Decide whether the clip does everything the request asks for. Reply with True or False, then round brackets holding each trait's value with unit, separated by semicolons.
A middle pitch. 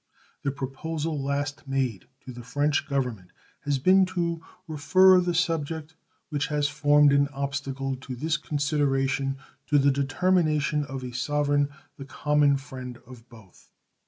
True (145 Hz)